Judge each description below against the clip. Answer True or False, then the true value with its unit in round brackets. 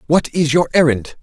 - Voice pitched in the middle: True (150 Hz)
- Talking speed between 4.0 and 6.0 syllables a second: True (5.0 syllables/s)